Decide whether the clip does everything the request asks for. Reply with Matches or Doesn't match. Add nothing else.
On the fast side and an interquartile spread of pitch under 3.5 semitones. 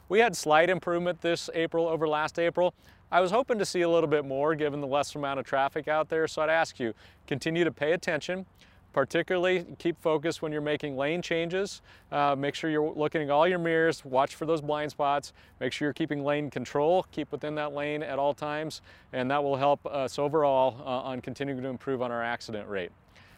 Matches